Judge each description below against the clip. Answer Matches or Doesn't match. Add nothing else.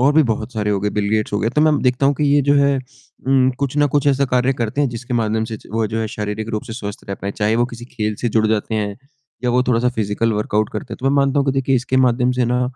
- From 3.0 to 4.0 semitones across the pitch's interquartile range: Matches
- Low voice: Matches